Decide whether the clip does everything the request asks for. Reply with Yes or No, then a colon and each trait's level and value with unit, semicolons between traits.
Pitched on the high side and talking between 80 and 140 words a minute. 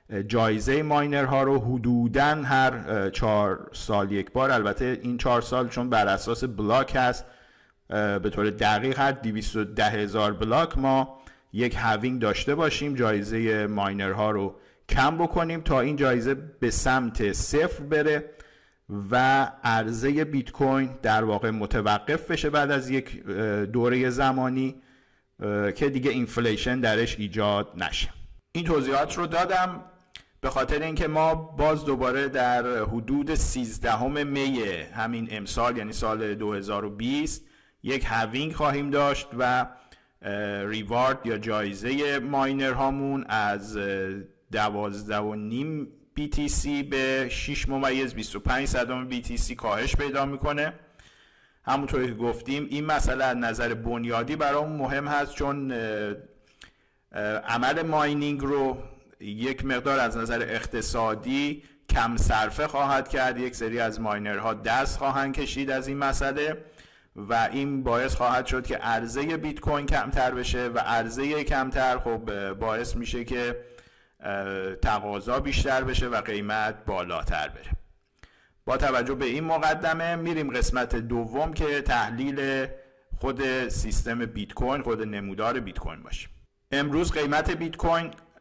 No: low, 125 Hz; average, 125 wpm